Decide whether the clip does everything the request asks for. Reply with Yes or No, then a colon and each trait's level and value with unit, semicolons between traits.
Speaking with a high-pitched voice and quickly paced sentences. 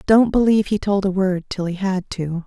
Yes: high, 195 Hz; fast, 245 wpm